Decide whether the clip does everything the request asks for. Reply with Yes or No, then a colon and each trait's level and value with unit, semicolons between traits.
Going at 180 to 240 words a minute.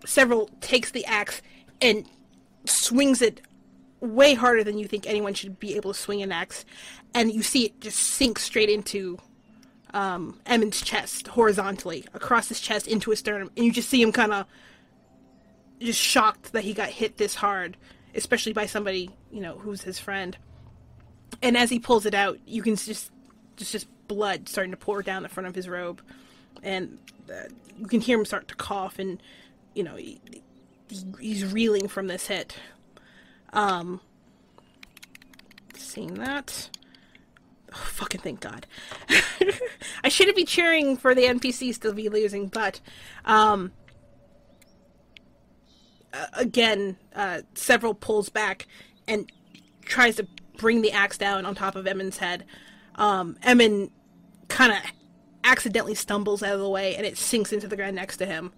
No: average, 160 wpm